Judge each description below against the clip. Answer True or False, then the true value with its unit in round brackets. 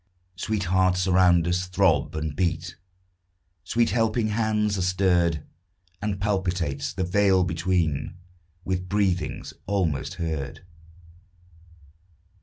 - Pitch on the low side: True (90 Hz)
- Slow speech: True (100 wpm)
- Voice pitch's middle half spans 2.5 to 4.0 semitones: True (2.9 semitones)